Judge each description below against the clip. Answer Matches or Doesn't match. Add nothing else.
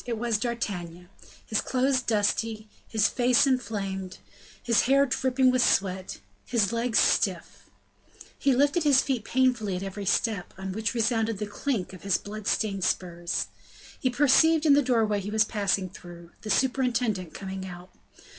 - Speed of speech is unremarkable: Matches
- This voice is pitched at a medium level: Doesn't match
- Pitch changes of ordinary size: Matches